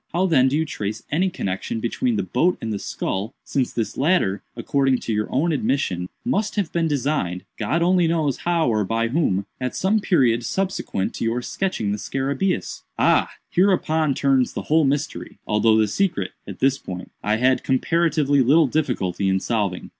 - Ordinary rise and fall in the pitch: No, wide, 7.2 semitones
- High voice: No, low, 135 Hz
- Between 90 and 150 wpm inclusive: No, average, 175 wpm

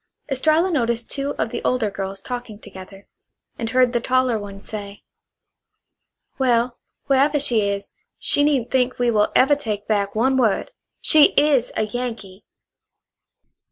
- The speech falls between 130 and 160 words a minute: Yes, average, 145 wpm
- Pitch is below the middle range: No, high, 240 Hz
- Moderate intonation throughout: Yes, average, 4.1 semitones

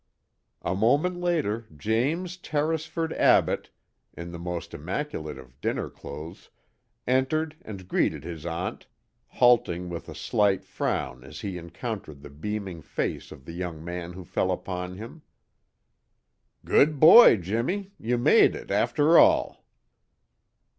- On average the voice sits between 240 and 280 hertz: No, low, 100 Hz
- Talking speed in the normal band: No, slow, 130 wpm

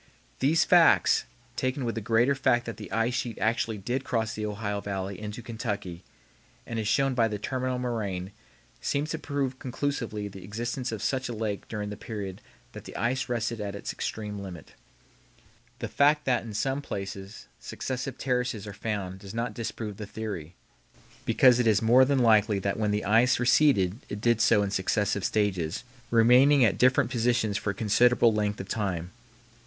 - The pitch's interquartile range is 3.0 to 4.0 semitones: Yes, average, 3.4 semitones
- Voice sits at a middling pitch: No, low, 110 Hz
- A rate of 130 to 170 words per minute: No, average, 180 wpm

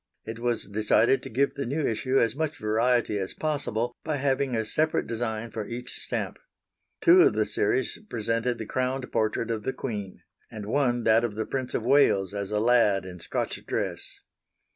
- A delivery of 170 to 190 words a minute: Yes, average, 185 wpm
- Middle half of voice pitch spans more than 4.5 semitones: No, average, 3.7 semitones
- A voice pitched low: Yes, low, 115 Hz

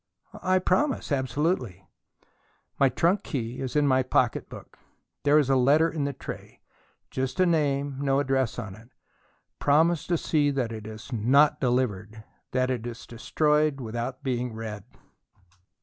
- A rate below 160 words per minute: Yes, average, 150 wpm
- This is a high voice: No, low, 135 Hz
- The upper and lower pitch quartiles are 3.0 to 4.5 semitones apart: Yes, average, 3.8 semitones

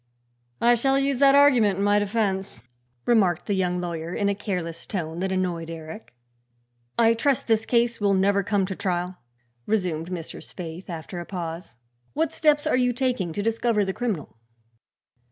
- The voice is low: No, high, 195 Hz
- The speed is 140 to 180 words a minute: Yes, average, 170 wpm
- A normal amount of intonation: Yes, average, 4.8 semitones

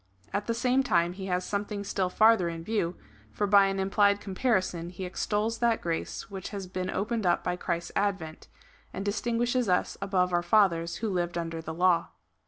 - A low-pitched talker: No, high, 190 Hz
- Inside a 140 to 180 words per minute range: No, average, 190 wpm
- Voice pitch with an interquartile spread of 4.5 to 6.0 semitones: No, average, 3.2 semitones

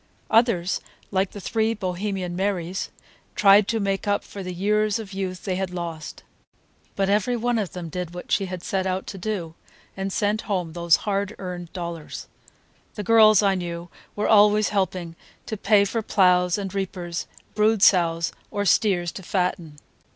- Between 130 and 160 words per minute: No, average, 170 wpm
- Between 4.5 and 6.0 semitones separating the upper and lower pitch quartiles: No, average, 2.7 semitones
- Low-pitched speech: No, high, 195 Hz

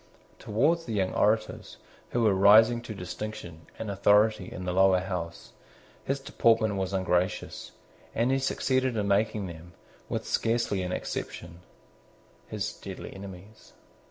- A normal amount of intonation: Yes, average, 3.4 semitones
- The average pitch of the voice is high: No, low, 100 Hz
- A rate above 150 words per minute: No, slow, 135 wpm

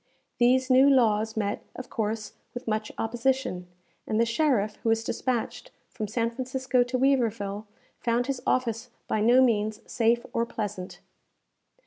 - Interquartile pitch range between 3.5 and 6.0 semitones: No, average, 2.8 semitones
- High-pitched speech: Yes, high, 230 Hz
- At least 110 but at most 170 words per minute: Yes, average, 145 wpm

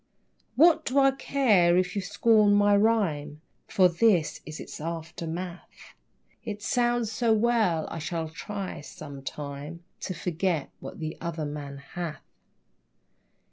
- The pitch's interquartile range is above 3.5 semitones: Yes, wide, 5.4 semitones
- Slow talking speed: Yes, slow, 130 wpm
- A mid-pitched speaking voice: Yes, medium, 180 Hz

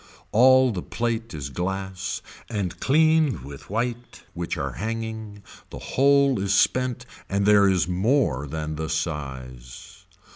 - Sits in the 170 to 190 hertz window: No, low, 100 Hz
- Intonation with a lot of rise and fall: Yes, wide, 7.4 semitones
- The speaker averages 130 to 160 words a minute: Yes, slow, 135 wpm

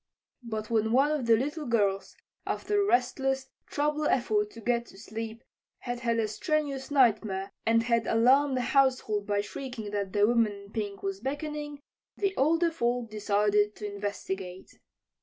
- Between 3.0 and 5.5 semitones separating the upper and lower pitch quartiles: Yes, average, 4.4 semitones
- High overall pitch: Yes, high, 230 Hz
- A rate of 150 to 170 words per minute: Yes, average, 160 wpm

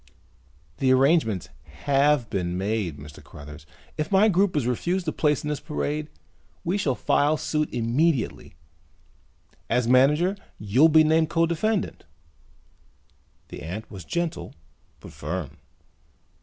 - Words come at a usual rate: No, slow, 130 wpm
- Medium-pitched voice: Yes, medium, 145 Hz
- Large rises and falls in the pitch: Yes, wide, 7.3 semitones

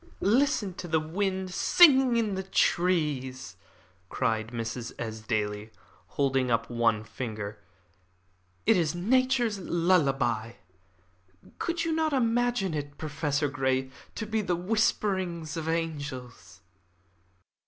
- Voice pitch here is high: No, medium, 160 Hz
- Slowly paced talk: Yes, slow, 110 wpm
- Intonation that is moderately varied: No, wide, 8.2 semitones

